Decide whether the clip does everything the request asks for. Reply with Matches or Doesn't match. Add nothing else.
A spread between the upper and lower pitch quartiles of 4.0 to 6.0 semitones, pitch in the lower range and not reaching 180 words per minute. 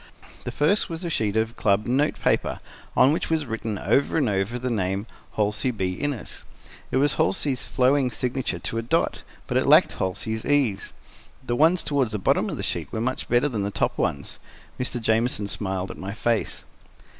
Doesn't match